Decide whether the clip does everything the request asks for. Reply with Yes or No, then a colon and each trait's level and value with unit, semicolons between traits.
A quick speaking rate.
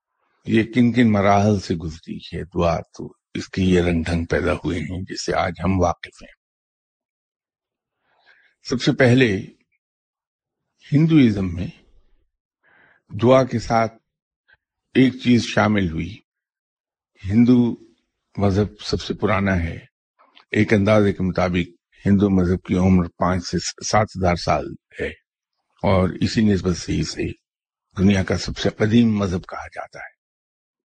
No: slow, 130 wpm